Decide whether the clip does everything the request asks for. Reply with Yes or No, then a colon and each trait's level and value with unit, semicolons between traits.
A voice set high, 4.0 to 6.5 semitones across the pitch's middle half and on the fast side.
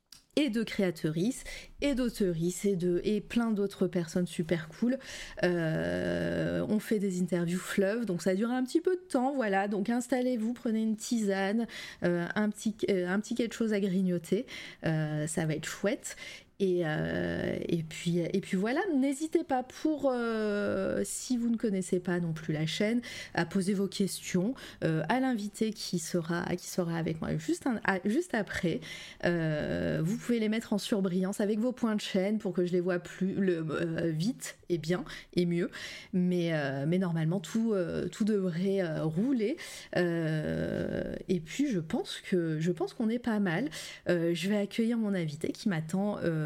No: high, 195 Hz; average, 4.4 semitones; average, 185 wpm